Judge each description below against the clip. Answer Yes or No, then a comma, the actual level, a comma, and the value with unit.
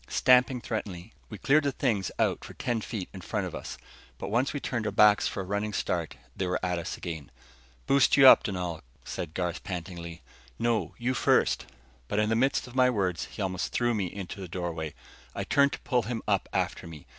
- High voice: No, low, 100 Hz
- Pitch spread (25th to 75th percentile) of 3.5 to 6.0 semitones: Yes, average, 5.2 semitones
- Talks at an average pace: No, fast, 215 wpm